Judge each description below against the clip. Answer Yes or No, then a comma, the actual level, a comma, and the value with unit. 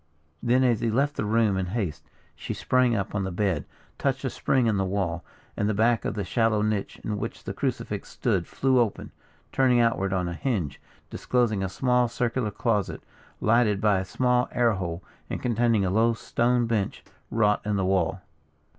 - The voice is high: No, low, 110 Hz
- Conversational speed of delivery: Yes, average, 190 wpm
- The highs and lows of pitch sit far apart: No, average, 3.6 semitones